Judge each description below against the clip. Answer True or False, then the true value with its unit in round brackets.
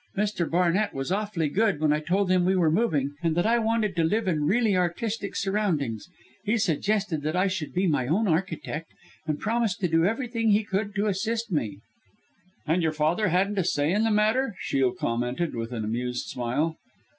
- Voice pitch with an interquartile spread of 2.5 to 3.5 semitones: False (5.5 semitones)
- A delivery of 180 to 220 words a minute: True (195 wpm)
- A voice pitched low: False (180 Hz)